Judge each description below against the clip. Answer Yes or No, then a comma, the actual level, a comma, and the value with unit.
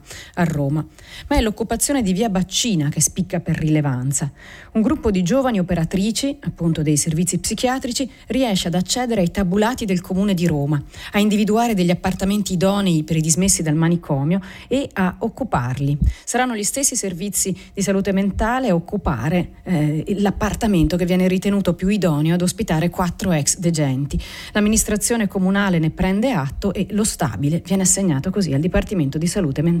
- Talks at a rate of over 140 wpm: Yes, average, 160 wpm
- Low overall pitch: No, medium, 185 Hz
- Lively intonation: No, average, 4.1 semitones